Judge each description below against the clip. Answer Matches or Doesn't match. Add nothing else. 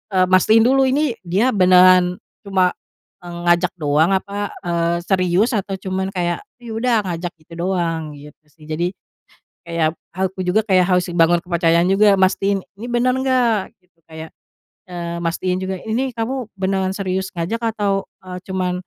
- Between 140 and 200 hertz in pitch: Matches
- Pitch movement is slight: Doesn't match